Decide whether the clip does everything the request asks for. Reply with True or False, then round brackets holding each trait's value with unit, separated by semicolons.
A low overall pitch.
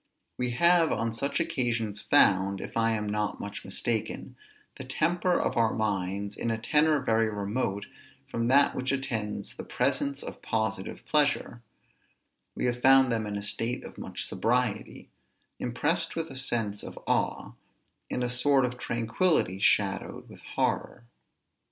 True (115 Hz)